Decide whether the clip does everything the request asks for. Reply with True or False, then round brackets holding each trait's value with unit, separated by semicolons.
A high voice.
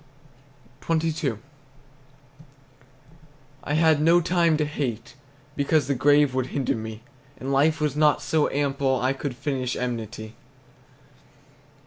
False (140 Hz)